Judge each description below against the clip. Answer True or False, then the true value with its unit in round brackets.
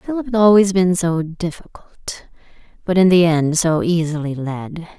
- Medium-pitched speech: True (175 Hz)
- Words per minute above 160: False (155 wpm)